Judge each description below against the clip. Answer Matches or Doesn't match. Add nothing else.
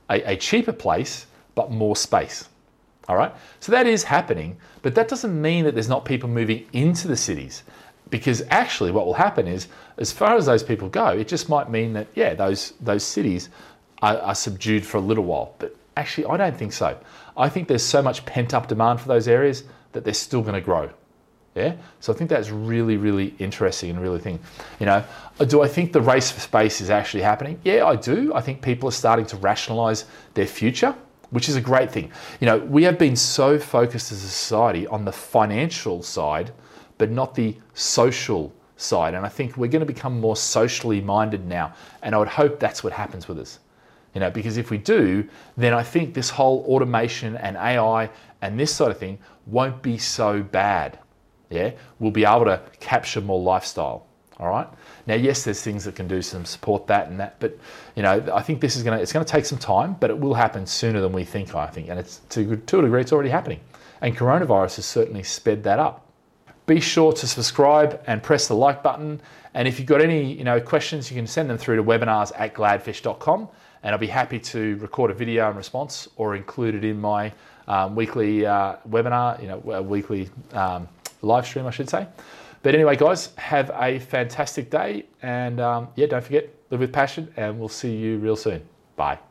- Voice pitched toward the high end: Doesn't match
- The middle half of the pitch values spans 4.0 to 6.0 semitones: Matches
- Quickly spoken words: Matches